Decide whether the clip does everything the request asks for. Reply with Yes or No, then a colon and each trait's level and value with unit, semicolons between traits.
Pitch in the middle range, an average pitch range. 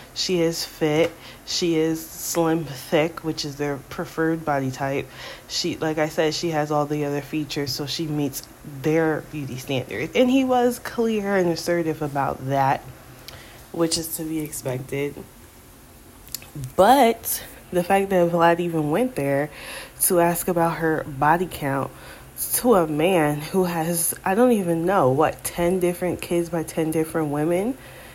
Yes: medium, 160 Hz; average, 3.0 semitones